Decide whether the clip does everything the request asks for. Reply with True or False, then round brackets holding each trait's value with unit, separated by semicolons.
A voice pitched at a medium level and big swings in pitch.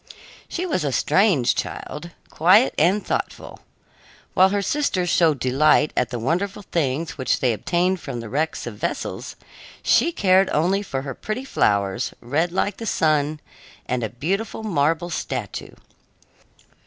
True (160 Hz; 6.4 semitones)